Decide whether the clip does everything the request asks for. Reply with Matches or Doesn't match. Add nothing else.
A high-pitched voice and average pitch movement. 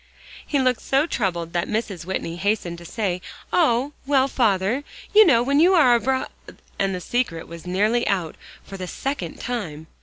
Doesn't match